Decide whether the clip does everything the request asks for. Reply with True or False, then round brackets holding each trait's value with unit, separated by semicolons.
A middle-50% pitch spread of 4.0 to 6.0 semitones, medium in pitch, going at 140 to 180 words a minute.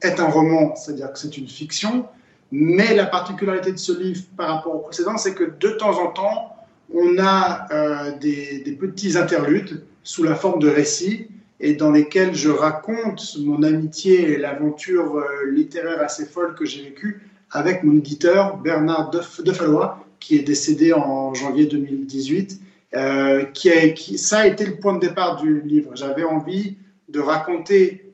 True (4.4 semitones; 170 Hz; 175 wpm)